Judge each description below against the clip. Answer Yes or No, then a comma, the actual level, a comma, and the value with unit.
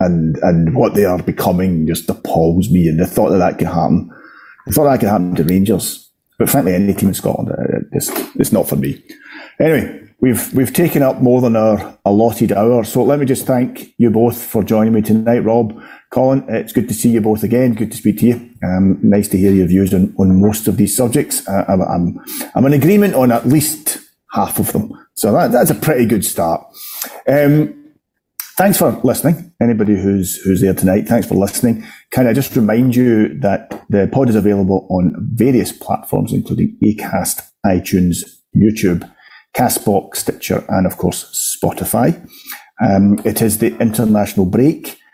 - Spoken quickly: No, average, 190 wpm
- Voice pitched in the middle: No, low, 110 Hz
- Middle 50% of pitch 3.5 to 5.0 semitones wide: Yes, average, 4.2 semitones